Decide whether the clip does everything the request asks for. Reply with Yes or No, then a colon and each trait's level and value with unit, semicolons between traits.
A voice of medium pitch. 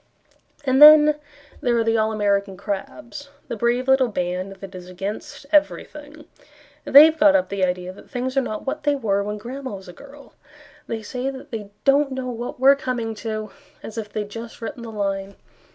No: high, 230 Hz